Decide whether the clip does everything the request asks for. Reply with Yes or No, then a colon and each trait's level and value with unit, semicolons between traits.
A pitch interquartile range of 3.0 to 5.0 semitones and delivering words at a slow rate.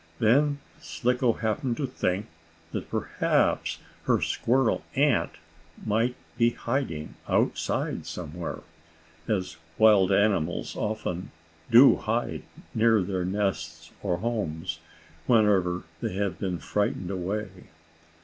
Yes: average, 4.6 semitones; slow, 105 wpm